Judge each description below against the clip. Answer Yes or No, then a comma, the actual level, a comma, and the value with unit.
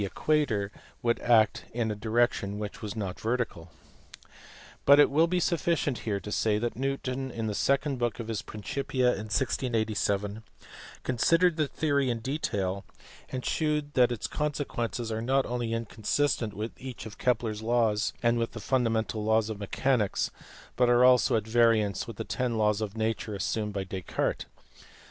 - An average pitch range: Yes, average, 3.2 semitones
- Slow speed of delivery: No, average, 165 wpm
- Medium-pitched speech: No, low, 115 Hz